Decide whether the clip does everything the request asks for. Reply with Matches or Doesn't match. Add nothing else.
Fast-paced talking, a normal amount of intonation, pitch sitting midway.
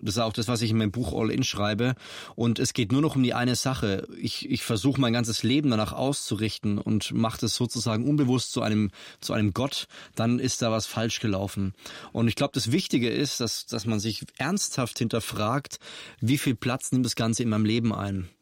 Doesn't match